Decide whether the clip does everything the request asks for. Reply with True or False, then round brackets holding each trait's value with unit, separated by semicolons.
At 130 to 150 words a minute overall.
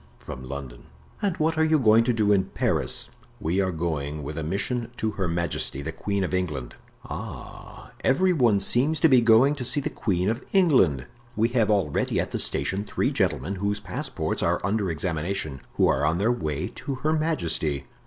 False (195 wpm)